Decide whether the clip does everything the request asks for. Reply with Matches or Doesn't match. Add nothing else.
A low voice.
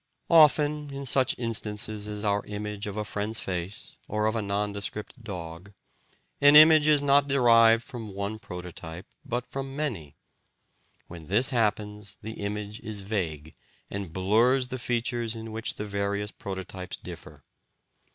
Matches